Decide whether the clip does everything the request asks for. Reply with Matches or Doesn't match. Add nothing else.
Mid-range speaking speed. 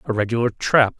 Matches